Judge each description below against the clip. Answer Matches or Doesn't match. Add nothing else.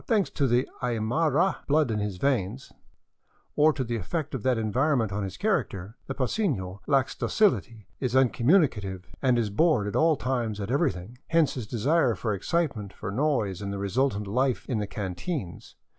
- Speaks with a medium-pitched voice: Doesn't match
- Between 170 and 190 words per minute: Matches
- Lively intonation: Matches